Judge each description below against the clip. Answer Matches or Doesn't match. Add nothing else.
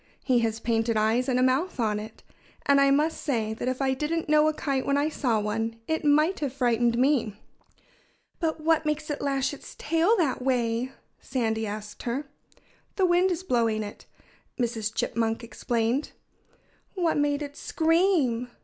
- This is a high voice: Matches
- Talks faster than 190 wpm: Doesn't match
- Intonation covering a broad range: Doesn't match